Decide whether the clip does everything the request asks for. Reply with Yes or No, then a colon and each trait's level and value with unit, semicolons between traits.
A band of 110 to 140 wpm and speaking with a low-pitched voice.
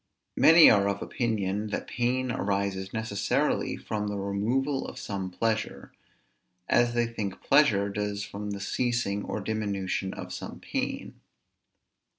Yes: slow, 135 wpm; low, 105 Hz